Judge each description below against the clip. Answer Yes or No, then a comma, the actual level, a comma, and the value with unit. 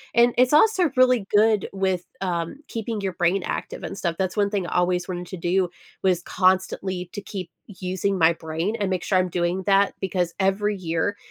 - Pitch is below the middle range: No, high, 190 Hz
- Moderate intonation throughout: No, narrow, 2.3 semitones